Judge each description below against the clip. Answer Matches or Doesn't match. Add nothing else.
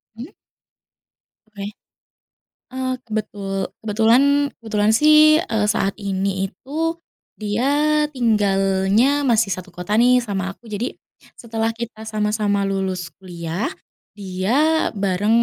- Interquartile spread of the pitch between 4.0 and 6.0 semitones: Matches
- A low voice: Doesn't match